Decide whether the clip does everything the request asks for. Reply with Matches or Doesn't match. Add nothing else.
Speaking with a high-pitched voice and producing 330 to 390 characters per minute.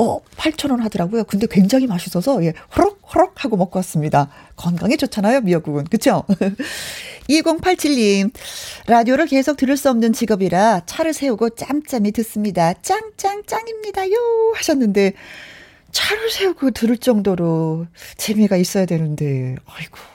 Doesn't match